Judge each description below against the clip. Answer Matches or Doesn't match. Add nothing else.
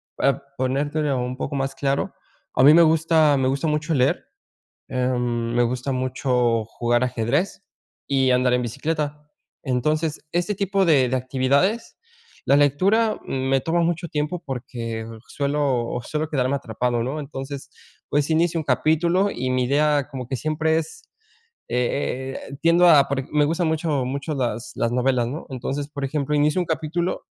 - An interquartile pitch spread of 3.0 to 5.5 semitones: Matches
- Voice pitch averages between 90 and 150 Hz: Matches